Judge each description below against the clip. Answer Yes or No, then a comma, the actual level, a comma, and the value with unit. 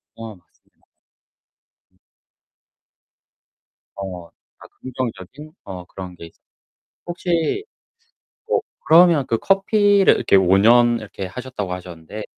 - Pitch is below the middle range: Yes, low, 115 Hz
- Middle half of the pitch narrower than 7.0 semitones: No, wide, 9.0 semitones